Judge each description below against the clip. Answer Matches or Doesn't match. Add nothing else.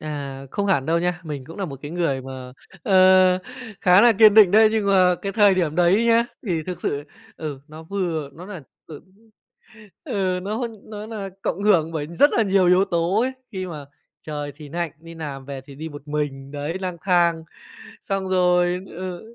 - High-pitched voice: Doesn't match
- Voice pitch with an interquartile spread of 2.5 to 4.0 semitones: Doesn't match